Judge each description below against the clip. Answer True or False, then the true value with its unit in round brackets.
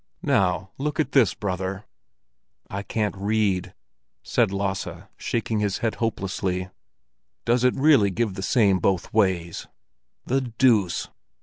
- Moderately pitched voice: False (100 Hz)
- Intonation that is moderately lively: True (3.4 semitones)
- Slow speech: True (125 wpm)